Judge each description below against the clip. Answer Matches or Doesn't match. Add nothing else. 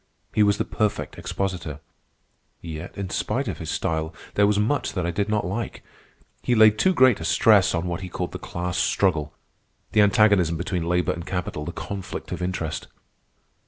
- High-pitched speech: Doesn't match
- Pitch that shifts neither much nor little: Matches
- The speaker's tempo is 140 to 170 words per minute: Doesn't match